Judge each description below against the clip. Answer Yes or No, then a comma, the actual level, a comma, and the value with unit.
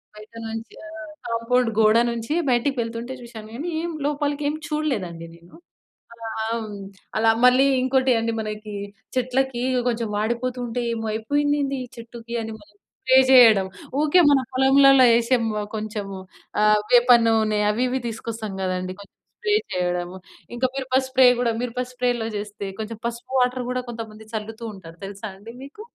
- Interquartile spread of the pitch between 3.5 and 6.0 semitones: No, average, 3.0 semitones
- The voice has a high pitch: Yes, high, 230 Hz